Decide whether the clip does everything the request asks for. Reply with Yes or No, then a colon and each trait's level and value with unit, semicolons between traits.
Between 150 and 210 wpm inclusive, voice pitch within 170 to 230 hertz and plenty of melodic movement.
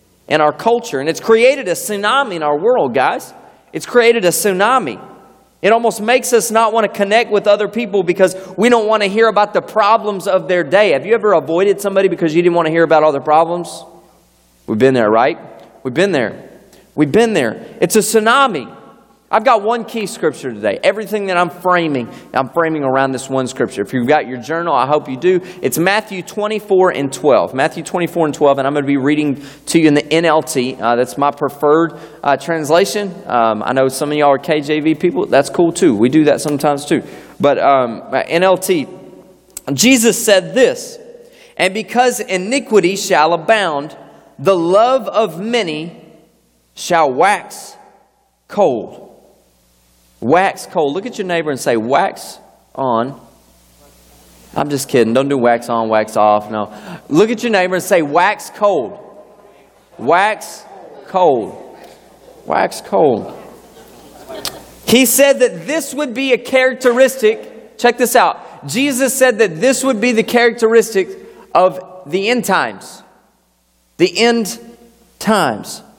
Yes: average, 165 wpm; medium, 185 Hz; wide, 7.8 semitones